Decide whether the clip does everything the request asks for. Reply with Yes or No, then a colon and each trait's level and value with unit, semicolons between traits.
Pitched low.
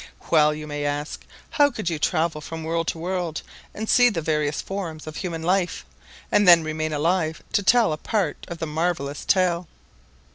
No: medium, 165 Hz